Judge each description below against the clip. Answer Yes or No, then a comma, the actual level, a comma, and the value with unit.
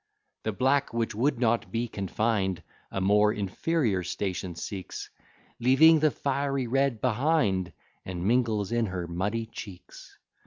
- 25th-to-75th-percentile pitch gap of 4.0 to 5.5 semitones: Yes, average, 5.1 semitones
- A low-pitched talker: Yes, low, 115 Hz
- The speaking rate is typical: No, slow, 130 wpm